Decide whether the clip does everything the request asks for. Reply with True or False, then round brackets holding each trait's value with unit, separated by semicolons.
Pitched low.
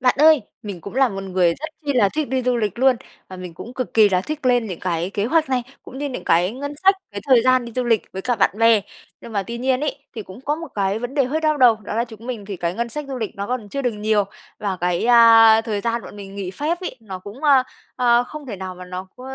False (230 Hz)